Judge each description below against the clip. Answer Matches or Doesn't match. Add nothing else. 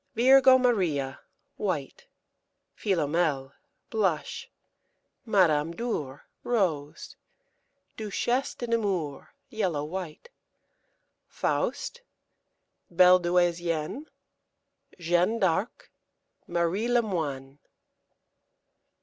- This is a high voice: Doesn't match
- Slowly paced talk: Matches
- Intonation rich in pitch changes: Matches